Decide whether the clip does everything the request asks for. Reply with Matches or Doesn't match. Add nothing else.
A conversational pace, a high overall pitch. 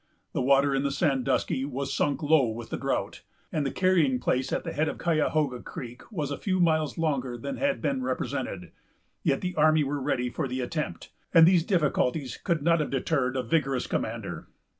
Doesn't match